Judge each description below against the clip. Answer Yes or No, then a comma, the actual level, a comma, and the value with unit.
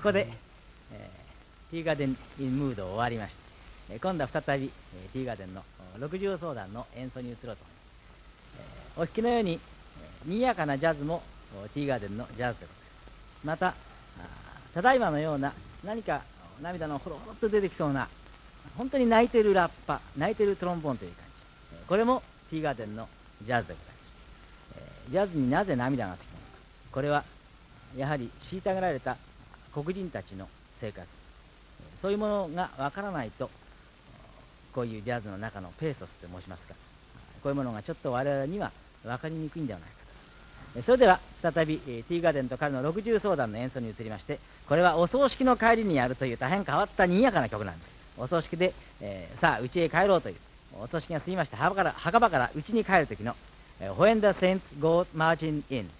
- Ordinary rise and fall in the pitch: No, wide, 7.7 semitones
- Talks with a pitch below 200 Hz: Yes, medium, 140 Hz